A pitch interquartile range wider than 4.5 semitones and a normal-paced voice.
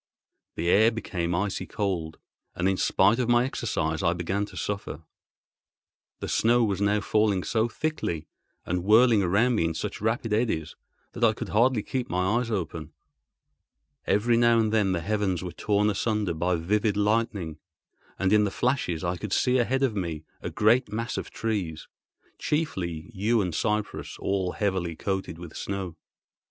No: average, 4.2 semitones; average, 170 wpm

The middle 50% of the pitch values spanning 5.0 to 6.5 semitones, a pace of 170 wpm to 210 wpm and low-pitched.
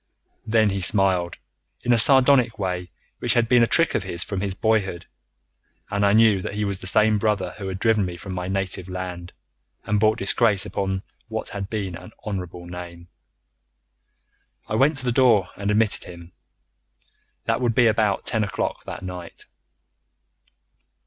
No: average, 3.2 semitones; average, 175 wpm; low, 100 Hz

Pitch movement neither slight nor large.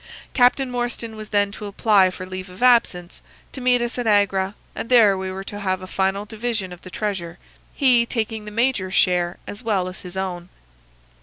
Yes: average, 3.8 semitones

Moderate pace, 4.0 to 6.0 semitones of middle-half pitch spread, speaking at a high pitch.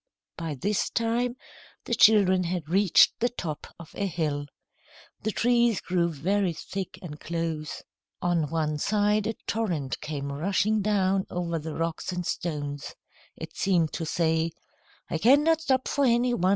No: average, 150 wpm; average, 4.8 semitones; medium, 180 Hz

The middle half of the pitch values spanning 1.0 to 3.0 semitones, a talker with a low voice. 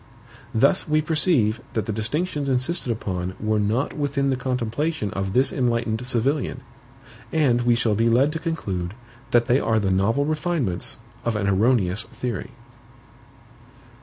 No: average, 4.8 semitones; low, 120 Hz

